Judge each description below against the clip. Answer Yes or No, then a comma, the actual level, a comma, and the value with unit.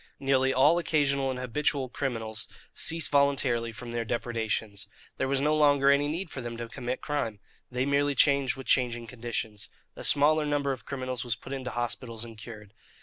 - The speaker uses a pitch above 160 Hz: No, low, 130 Hz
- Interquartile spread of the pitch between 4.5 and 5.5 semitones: No, average, 3.2 semitones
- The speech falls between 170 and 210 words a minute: Yes, average, 180 wpm